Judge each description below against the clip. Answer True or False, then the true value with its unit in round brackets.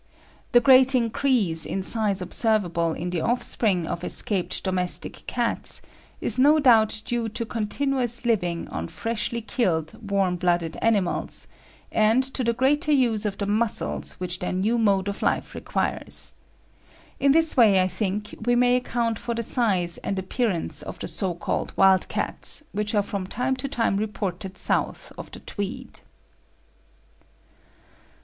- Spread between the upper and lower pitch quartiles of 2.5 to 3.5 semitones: False (4.3 semitones)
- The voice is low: False (215 Hz)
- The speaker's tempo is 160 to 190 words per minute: False (150 wpm)